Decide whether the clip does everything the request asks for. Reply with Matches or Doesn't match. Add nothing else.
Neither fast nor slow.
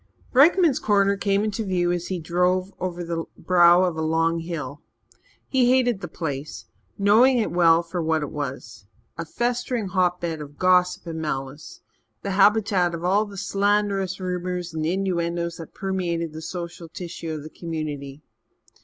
Matches